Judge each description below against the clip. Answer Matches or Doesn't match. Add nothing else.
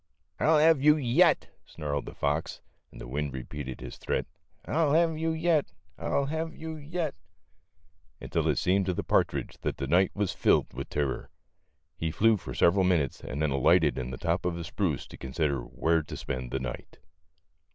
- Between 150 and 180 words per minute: Doesn't match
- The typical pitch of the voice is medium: Doesn't match